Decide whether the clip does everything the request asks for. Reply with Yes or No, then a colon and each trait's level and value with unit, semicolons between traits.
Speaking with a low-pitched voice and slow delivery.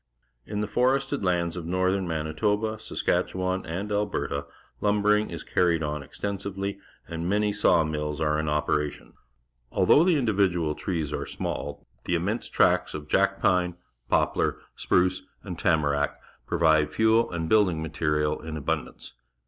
Yes: very low, 90 Hz; slow, 130 wpm